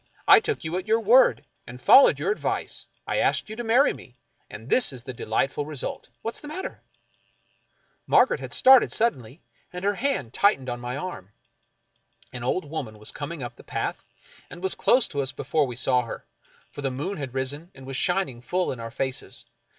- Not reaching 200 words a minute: No, fast, 205 wpm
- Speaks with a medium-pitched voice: Yes, medium, 145 Hz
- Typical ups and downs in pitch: No, wide, 7.9 semitones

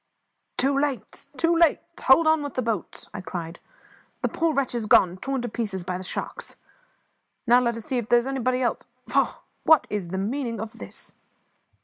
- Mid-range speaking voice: No, high, 240 Hz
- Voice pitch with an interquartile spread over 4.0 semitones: Yes, average, 4.7 semitones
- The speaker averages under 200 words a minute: No, fast, 205 wpm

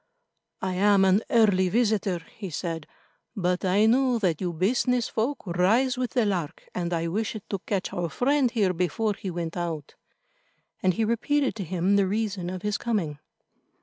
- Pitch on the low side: No, high, 195 Hz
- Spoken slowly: No, average, 175 wpm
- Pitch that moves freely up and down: No, average, 4.0 semitones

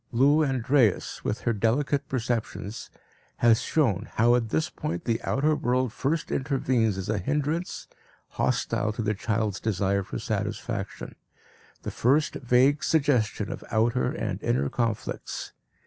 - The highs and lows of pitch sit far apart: No, average, 4.2 semitones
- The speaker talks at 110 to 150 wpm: Yes, slow, 135 wpm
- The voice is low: Yes, low, 120 Hz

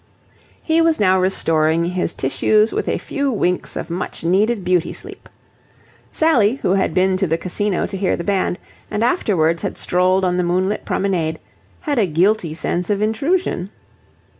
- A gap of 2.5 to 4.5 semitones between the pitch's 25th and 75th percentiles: Yes, average, 3.4 semitones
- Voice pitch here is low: No, medium, 185 Hz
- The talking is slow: No, average, 165 wpm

